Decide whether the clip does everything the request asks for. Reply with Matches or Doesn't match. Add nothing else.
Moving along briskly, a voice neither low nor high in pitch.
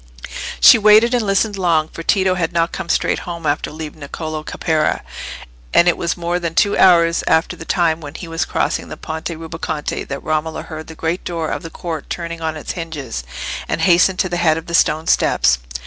Matches